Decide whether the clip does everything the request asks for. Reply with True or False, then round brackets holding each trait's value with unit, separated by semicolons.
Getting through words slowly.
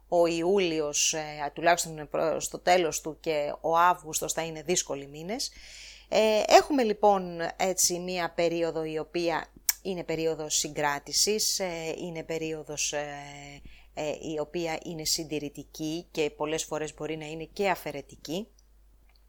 True (115 wpm)